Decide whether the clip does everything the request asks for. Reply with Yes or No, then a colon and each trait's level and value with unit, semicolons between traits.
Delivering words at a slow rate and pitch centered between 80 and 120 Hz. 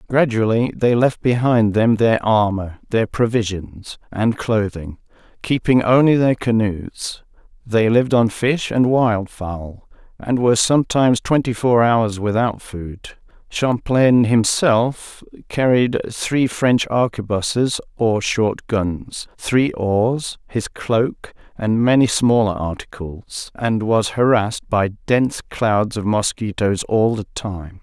Yes: slow, 125 wpm; low, 115 Hz